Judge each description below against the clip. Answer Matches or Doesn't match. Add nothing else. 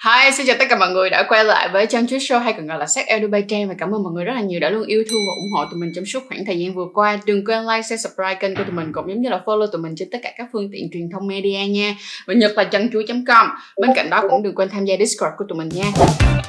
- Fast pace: Matches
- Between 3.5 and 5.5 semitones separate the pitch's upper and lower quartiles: Doesn't match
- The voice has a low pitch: Doesn't match